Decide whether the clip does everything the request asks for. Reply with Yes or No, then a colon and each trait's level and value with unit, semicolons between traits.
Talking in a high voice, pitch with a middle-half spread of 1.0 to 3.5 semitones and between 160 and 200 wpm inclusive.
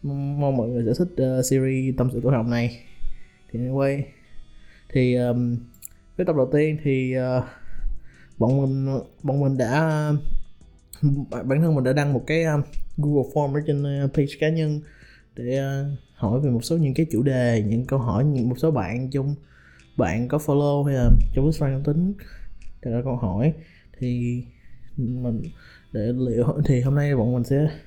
No: low, 130 Hz; average, 3.2 semitones; average, 185 wpm